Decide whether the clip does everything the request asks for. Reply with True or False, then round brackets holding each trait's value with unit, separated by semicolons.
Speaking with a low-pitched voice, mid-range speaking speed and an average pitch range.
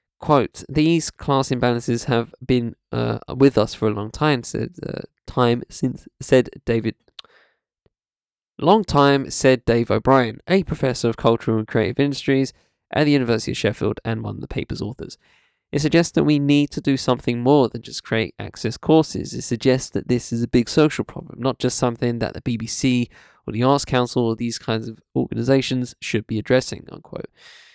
True (125 Hz; 180 wpm; 3.5 semitones)